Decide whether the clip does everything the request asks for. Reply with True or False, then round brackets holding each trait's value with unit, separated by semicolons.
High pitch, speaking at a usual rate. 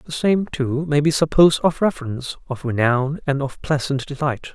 False (145 Hz; 185 wpm)